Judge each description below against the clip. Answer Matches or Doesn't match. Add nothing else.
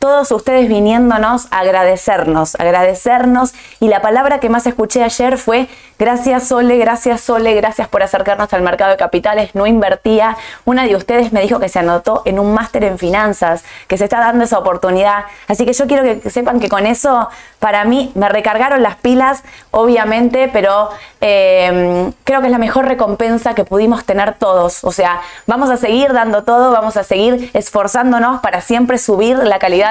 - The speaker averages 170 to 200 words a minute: Matches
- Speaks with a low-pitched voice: Doesn't match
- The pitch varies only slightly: Doesn't match